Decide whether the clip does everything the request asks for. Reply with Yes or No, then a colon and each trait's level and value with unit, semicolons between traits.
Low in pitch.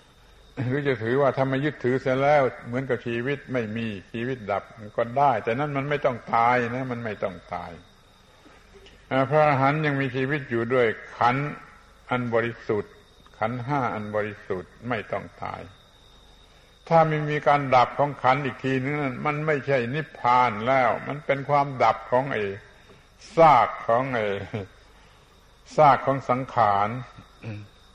Yes: low, 130 Hz